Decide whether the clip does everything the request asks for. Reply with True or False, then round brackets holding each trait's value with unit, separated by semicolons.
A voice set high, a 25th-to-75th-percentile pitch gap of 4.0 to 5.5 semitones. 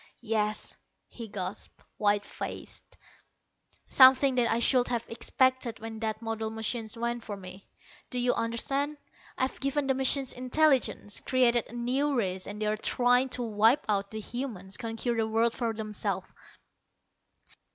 False (230 Hz; 2.9 semitones)